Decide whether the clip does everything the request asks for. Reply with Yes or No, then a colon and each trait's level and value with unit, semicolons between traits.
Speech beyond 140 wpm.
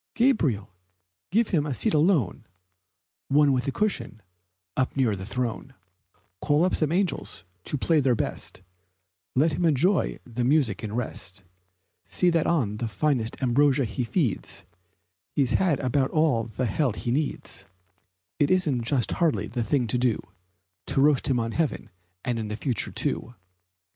Yes: average, 155 wpm